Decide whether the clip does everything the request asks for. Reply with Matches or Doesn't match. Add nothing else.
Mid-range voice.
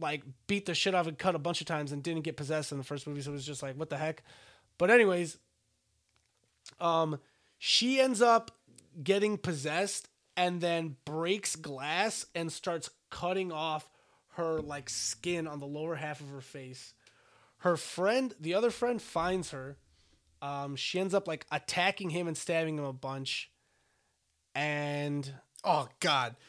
Matches